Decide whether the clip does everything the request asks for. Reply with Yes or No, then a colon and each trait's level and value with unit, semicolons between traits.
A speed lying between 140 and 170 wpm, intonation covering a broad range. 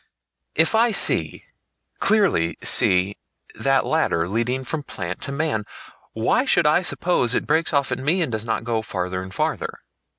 Yes: average, 165 wpm; wide, 8.0 semitones